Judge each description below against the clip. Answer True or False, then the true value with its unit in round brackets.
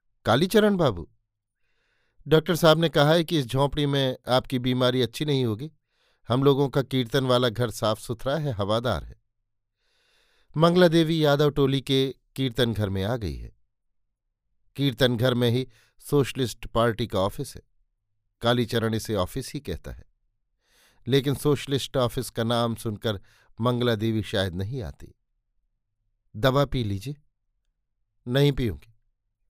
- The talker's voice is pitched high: False (120 Hz)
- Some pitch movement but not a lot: True (4.4 semitones)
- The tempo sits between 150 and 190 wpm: False (140 wpm)